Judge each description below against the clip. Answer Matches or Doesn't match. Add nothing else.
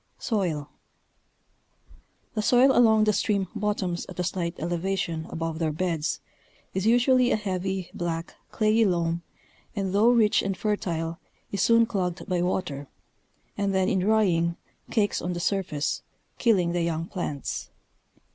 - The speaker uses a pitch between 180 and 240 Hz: Matches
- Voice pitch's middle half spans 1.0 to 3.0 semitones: Doesn't match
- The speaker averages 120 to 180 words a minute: Matches